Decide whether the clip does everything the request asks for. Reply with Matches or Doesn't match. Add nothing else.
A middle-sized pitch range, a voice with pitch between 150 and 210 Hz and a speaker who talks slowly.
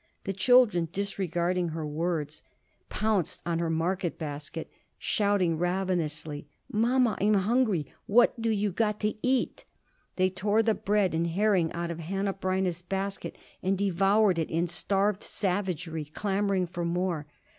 Doesn't match